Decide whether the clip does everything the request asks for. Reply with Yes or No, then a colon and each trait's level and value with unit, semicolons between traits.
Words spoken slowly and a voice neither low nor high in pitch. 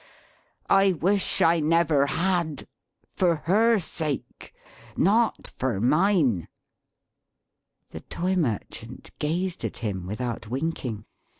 Yes: slow, 100 wpm; medium, 165 Hz